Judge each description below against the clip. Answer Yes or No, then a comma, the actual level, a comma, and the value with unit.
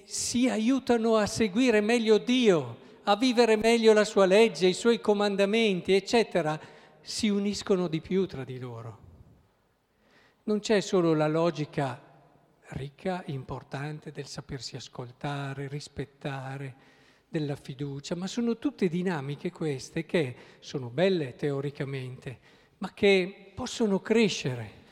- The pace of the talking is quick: No, average, 120 wpm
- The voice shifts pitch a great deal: Yes, wide, 7.0 semitones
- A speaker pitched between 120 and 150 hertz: No, medium, 170 Hz